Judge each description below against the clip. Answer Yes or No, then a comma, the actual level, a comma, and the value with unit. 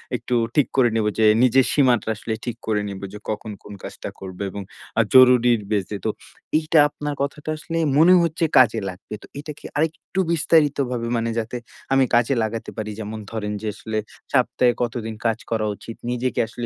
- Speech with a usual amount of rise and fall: Yes, average, 4.3 semitones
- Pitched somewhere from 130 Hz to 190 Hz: No, low, 120 Hz